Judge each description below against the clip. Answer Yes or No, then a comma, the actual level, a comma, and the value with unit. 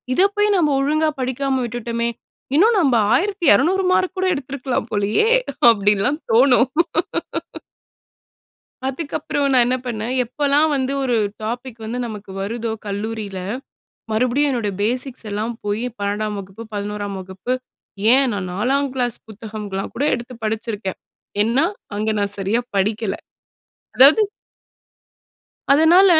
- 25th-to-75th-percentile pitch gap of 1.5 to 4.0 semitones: No, average, 4.8 semitones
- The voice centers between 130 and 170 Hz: No, high, 240 Hz